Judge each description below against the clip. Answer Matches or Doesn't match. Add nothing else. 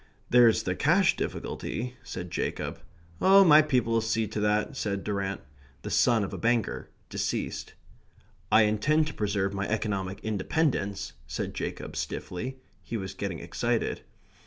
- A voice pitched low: Matches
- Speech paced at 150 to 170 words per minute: Doesn't match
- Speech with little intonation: Doesn't match